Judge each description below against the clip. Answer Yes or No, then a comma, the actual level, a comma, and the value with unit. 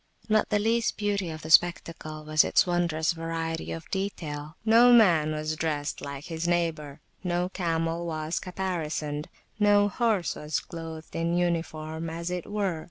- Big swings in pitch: No, average, 2.8 semitones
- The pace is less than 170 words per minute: Yes, average, 160 wpm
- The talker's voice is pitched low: No, medium, 165 Hz